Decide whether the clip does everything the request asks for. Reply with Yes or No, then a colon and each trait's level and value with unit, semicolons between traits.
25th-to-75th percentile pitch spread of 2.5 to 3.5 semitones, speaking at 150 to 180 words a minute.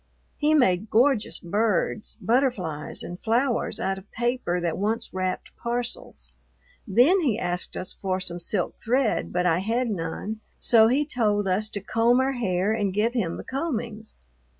No: average, 4.6 semitones; average, 160 wpm